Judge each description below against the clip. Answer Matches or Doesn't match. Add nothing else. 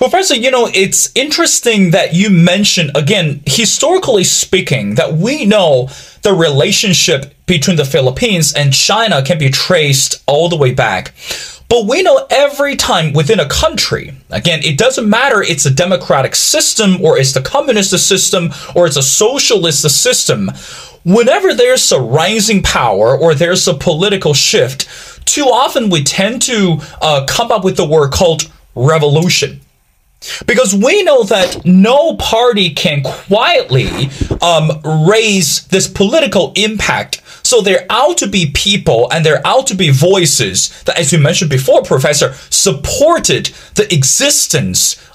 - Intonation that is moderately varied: Doesn't match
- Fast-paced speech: Doesn't match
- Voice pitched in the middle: Matches